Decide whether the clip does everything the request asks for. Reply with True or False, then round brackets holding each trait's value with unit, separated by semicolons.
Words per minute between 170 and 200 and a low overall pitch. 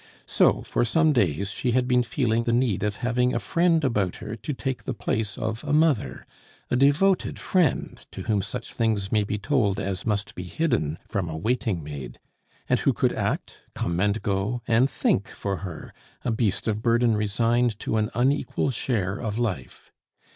True (185 wpm; 110 Hz)